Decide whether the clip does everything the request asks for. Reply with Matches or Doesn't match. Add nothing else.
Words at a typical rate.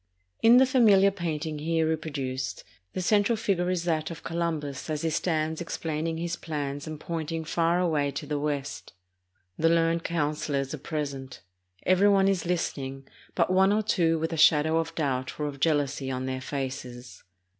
Matches